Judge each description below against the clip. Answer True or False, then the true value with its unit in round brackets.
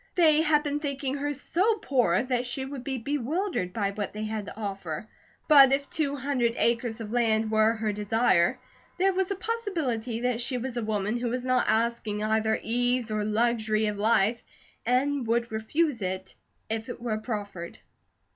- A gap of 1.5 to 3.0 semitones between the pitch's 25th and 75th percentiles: False (4.2 semitones)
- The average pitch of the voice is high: True (235 Hz)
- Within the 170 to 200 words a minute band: True (180 wpm)